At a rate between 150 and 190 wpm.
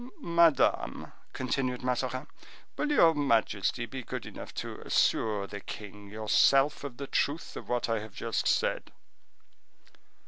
No: slow, 135 wpm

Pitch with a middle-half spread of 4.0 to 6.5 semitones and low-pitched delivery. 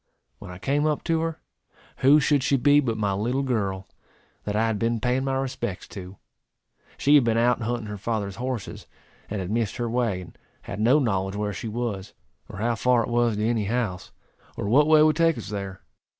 Yes: average, 4.3 semitones; low, 115 Hz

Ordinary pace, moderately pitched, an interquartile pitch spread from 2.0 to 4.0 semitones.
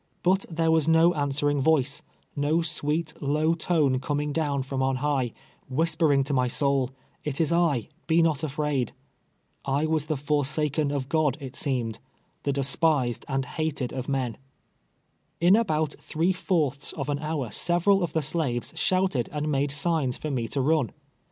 Yes: average, 170 wpm; medium, 145 Hz; average, 2.9 semitones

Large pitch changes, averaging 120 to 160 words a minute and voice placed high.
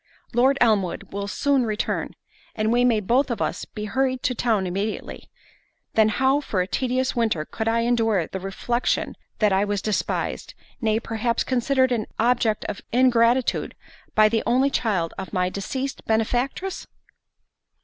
No: average, 3.2 semitones; average, 155 wpm; high, 230 Hz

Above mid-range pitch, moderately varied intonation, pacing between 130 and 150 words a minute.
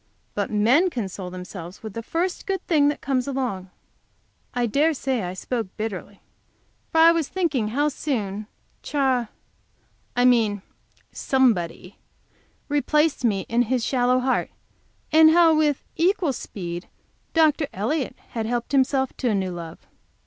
No: very high, 250 Hz; wide, 6.2 semitones; average, 140 wpm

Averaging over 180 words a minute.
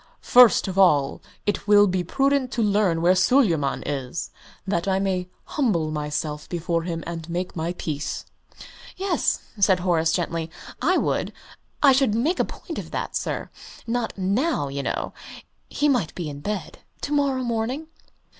No: average, 160 wpm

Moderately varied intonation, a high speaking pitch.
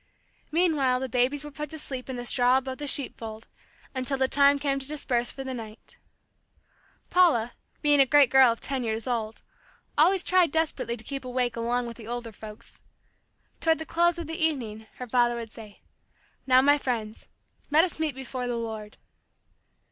Yes: average, 3.7 semitones; very high, 260 Hz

